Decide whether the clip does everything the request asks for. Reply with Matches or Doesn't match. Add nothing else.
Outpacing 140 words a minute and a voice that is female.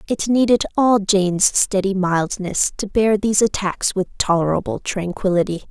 Doesn't match